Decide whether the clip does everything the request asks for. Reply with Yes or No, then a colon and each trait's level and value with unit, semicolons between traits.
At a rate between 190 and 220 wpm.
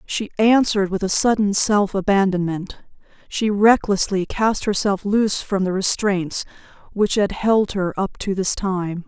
No: average, 150 wpm